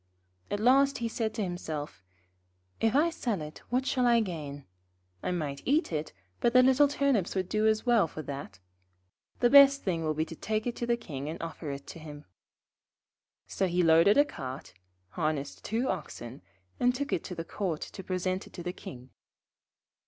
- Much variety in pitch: Yes, wide, 7.6 semitones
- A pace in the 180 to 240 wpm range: Yes, average, 190 wpm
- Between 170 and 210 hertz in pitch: Yes, medium, 185 Hz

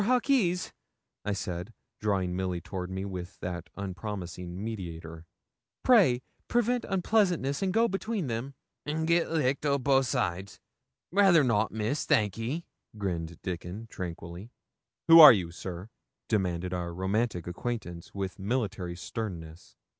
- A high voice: No, low, 105 Hz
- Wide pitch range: Yes, wide, 8.0 semitones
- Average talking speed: No, slow, 130 wpm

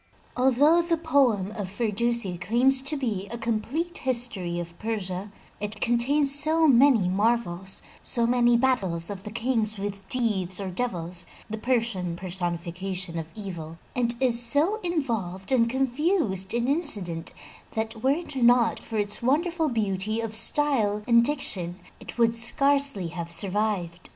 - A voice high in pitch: Yes, high, 225 Hz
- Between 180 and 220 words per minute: No, average, 145 wpm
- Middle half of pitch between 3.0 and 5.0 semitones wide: No, wide, 5.5 semitones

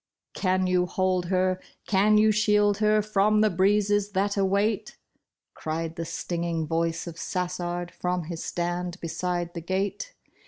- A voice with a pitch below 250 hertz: Yes, medium, 185 Hz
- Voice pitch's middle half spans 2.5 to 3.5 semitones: Yes, average, 2.8 semitones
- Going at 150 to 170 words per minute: Yes, average, 155 wpm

